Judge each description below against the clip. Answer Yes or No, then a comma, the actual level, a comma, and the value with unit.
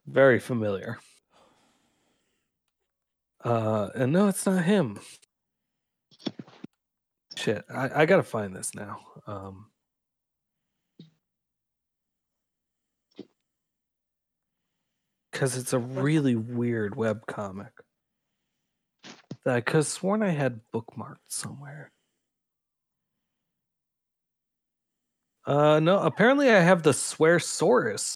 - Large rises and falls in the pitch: Yes, wide, 7.4 semitones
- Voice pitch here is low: Yes, low, 130 Hz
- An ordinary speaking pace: No, slow, 85 wpm